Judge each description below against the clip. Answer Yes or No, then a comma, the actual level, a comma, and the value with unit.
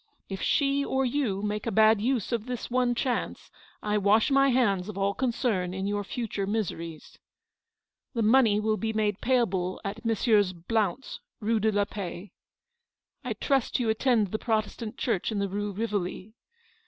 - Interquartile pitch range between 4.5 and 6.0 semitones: No, average, 3.2 semitones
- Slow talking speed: No, average, 175 wpm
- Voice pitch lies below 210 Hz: No, high, 215 Hz